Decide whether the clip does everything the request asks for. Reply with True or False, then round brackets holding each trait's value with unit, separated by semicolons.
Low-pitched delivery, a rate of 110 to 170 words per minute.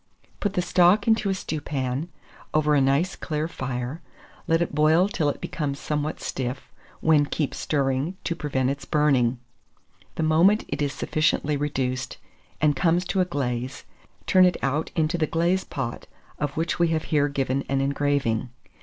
False (150 Hz; 165 wpm)